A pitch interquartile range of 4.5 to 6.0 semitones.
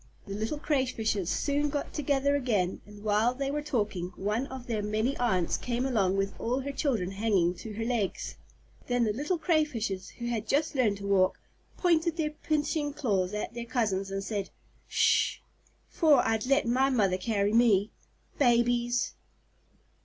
Yes: average, 5.2 semitones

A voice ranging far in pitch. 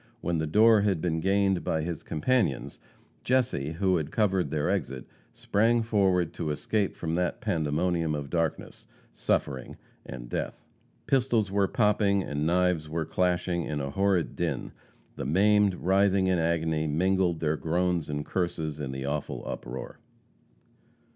No: average, 4.2 semitones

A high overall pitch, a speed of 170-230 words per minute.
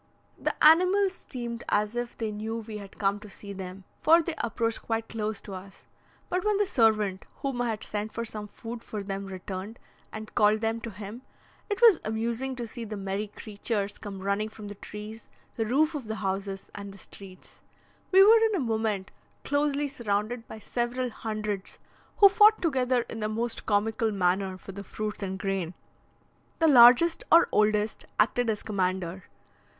Yes: high, 220 Hz; average, 180 wpm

